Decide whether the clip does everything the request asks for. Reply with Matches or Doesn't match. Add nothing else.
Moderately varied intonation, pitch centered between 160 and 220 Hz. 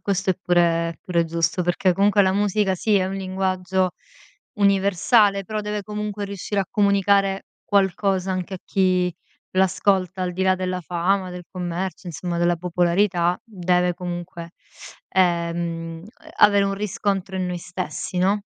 Doesn't match